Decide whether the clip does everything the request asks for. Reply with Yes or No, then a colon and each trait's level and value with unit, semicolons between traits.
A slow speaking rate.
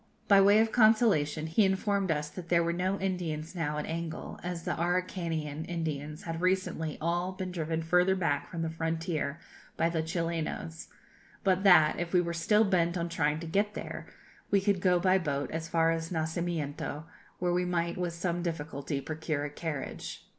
No: average, 180 wpm